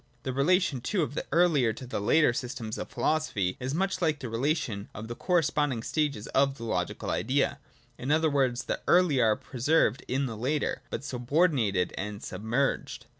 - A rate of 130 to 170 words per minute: No, average, 185 wpm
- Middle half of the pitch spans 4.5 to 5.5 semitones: Yes, average, 5.0 semitones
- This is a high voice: No, low, 130 Hz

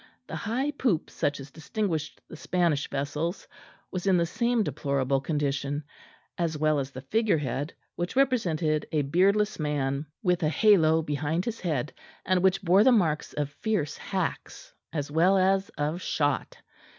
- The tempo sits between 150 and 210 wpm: Yes, average, 160 wpm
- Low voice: No, medium, 160 Hz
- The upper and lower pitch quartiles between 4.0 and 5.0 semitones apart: Yes, average, 4.7 semitones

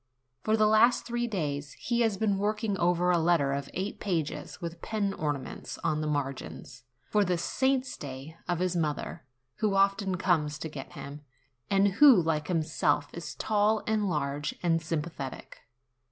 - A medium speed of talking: Yes, average, 165 wpm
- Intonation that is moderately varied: No, wide, 5.7 semitones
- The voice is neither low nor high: Yes, medium, 175 Hz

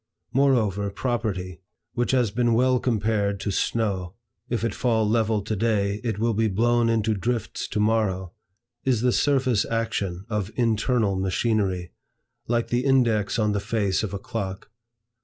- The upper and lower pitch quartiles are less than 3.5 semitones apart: Yes, average, 2.9 semitones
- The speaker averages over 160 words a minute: No, average, 155 wpm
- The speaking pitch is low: Yes, low, 110 Hz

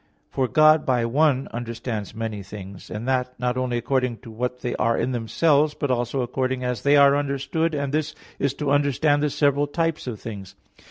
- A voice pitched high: No, low, 130 Hz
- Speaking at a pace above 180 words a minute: Yes, average, 195 wpm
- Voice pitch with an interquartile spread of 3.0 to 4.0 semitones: Yes, average, 3.3 semitones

